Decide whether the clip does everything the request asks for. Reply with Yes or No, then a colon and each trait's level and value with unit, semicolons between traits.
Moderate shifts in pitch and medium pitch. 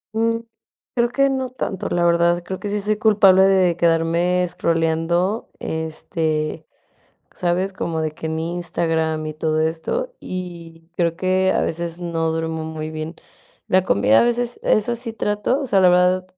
Yes: average, 3.2 semitones; medium, 175 Hz